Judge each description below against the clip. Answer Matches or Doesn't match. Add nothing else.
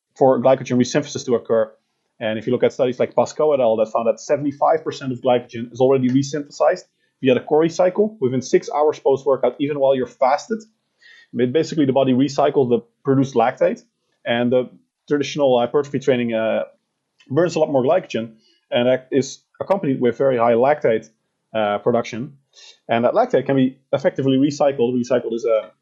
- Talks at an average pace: Matches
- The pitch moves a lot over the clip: Doesn't match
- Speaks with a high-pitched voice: Doesn't match